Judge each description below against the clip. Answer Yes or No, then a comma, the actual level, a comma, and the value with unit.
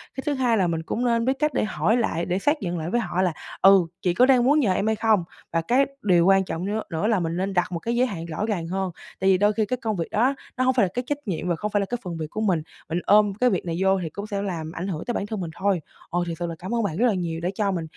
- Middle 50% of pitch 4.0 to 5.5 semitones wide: Yes, average, 4.7 semitones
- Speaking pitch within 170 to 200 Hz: Yes, high, 195 Hz